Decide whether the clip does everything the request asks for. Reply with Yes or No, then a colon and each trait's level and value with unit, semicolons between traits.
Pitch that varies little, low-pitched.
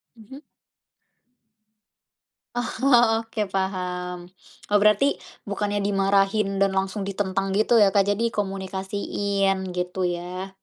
No: narrow, 1.4 semitones; high, 195 Hz